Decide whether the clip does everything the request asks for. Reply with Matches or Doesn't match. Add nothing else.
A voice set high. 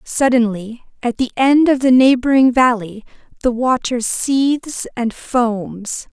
Matches